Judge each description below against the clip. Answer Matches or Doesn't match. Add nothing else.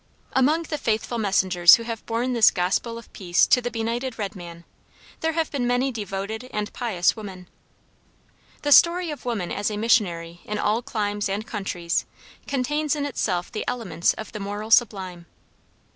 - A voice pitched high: Matches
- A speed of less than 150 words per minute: Doesn't match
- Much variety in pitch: Doesn't match